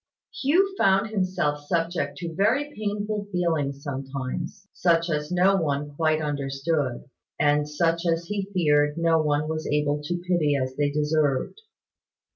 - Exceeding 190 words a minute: No, average, 140 wpm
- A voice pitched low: No, medium, 160 Hz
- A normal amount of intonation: Yes, average, 3.6 semitones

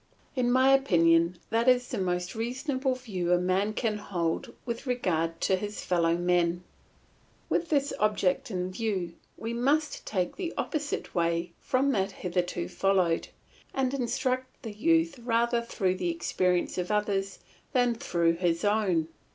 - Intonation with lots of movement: Yes, wide, 5.8 semitones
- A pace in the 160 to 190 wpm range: No, average, 150 wpm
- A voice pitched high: Yes, high, 205 Hz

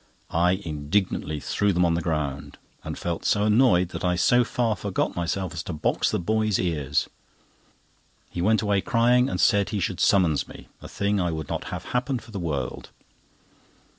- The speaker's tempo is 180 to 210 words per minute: Yes, average, 185 wpm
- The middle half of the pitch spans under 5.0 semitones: Yes, average, 4.2 semitones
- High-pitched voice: No, very low, 90 Hz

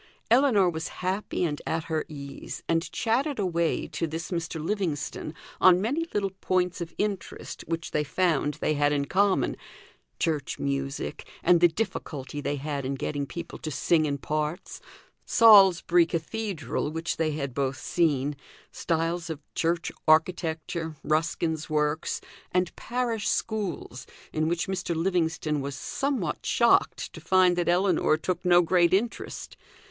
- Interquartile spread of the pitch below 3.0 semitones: No, average, 3.3 semitones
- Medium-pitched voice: Yes, medium, 165 Hz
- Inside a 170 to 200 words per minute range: No, average, 145 wpm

